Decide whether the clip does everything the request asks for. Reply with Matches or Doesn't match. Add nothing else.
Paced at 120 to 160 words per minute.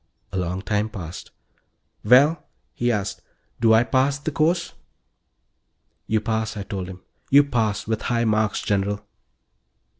Matches